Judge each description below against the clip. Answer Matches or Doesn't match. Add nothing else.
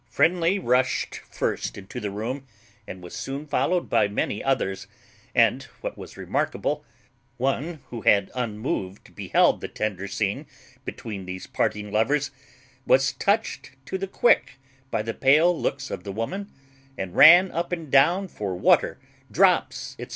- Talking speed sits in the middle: Matches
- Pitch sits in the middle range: Doesn't match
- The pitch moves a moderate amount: Doesn't match